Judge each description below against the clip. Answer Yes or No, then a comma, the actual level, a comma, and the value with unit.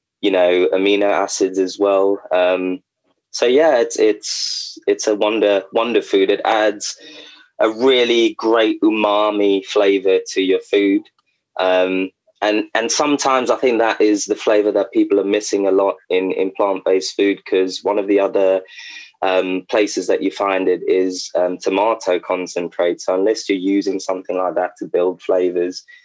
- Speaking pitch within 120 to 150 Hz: No, low, 100 Hz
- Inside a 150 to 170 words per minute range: Yes, average, 165 wpm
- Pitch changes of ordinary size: Yes, average, 3.2 semitones